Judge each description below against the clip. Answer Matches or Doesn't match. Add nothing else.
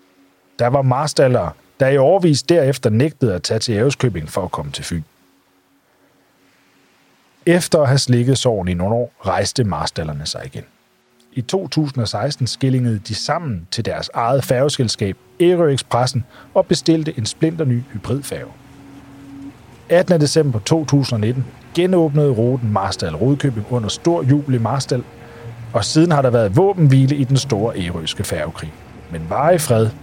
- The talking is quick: Doesn't match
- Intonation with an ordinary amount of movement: Matches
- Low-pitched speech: Matches